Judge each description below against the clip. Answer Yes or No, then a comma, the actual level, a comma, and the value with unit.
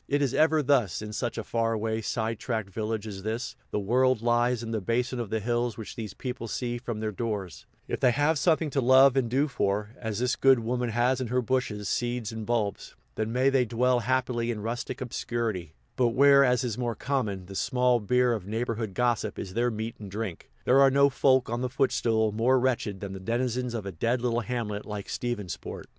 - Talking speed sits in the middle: No, fast, 215 wpm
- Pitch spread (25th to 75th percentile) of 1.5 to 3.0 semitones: Yes, narrow, 2.6 semitones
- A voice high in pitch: No, low, 120 Hz